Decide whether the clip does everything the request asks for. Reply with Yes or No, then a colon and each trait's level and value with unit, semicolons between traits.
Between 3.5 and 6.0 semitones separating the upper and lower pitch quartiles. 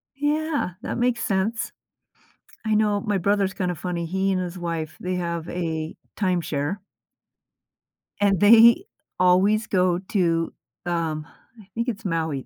Yes: average, 3.8 semitones